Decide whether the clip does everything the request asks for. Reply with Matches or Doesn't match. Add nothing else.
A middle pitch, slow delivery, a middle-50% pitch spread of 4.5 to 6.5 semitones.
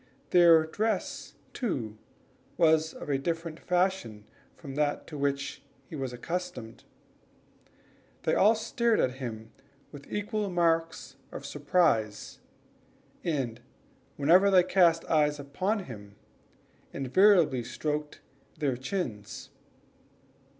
Matches